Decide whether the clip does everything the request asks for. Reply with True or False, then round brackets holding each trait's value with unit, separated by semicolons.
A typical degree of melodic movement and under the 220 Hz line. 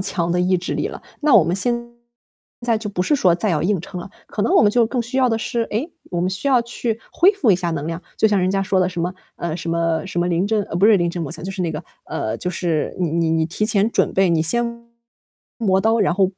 True (4.6 semitones; 190 Hz)